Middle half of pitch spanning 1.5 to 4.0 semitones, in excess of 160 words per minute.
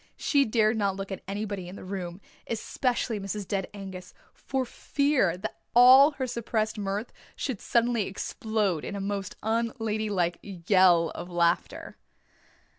No: average, 3.5 semitones; average, 145 wpm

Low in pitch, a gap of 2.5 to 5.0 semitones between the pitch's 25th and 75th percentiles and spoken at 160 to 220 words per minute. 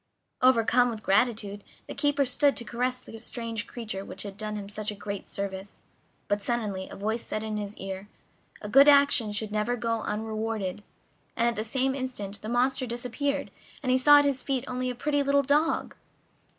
No: high, 230 Hz; average, 3.6 semitones; average, 190 wpm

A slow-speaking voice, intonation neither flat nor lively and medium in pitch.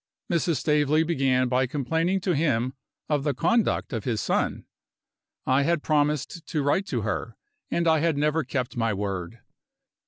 No: average, 160 wpm; average, 4.4 semitones; medium, 145 Hz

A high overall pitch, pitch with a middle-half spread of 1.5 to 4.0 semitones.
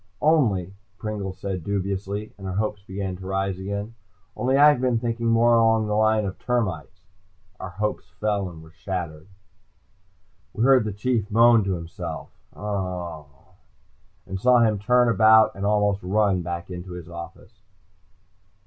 No: low, 100 Hz; average, 3.2 semitones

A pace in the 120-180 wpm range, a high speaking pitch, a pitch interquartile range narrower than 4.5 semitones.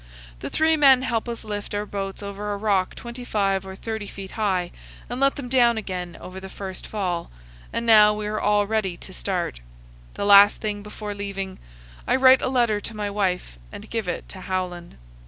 No: average, 195 wpm; high, 205 Hz; narrow, 2.6 semitones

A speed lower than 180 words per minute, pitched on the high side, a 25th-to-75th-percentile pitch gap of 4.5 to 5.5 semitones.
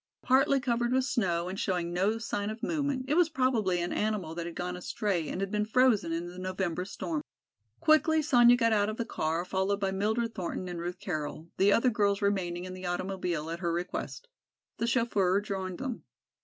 No: average, 195 wpm; high, 200 Hz; average, 4.9 semitones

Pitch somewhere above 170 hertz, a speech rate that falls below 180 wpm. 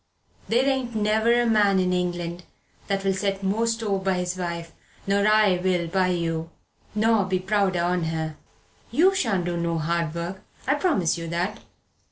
Yes: high, 190 Hz; average, 165 wpm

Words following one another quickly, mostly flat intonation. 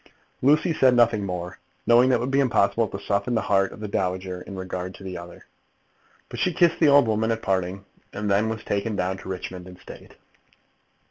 No: fast, 210 wpm; average, 4.2 semitones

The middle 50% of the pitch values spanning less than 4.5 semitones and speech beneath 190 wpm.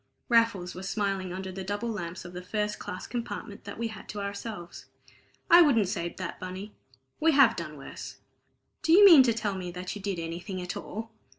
No: average, 3.9 semitones; average, 200 wpm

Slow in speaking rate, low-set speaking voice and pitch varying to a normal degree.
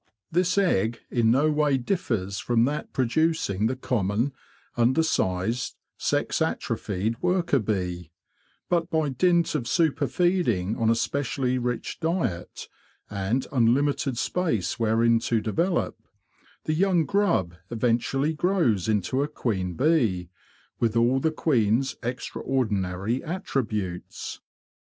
No: slow, 120 wpm; low, 125 Hz; wide, 6.3 semitones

